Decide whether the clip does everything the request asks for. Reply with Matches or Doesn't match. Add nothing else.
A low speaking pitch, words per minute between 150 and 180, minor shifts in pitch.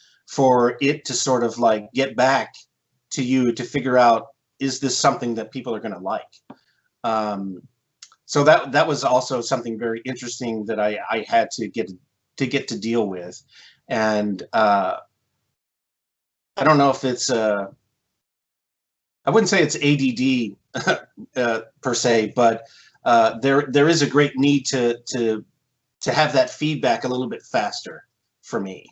Doesn't match